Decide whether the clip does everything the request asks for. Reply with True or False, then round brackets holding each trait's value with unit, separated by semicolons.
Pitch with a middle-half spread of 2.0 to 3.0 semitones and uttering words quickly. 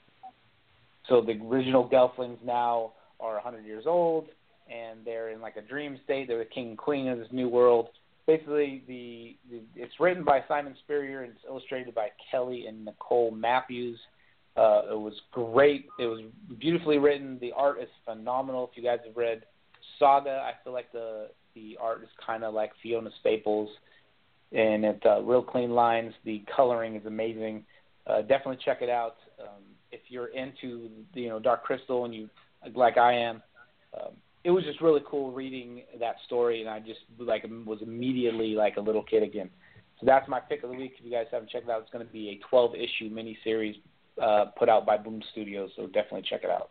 False (2.7 semitones; 195 wpm)